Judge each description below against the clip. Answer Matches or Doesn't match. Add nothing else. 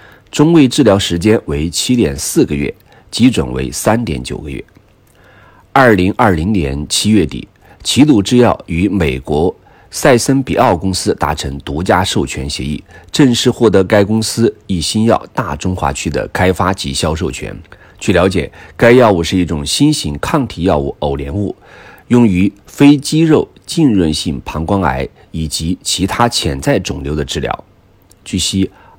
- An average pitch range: Doesn't match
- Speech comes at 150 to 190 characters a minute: Doesn't match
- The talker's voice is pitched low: Matches